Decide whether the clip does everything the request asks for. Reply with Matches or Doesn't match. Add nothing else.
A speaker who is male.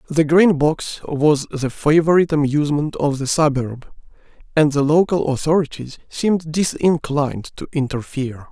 Matches